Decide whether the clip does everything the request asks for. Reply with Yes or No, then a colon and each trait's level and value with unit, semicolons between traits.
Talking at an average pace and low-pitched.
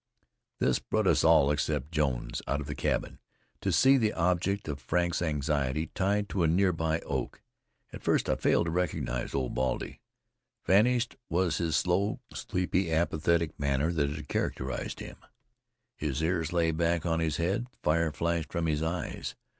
Yes: average, 160 wpm; very low, 80 Hz